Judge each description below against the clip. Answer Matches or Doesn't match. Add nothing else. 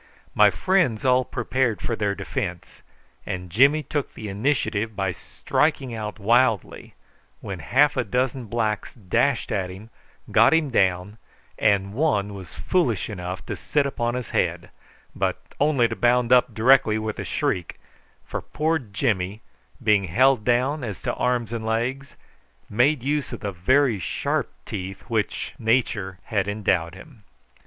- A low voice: Matches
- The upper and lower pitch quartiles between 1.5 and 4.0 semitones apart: Doesn't match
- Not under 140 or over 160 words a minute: Matches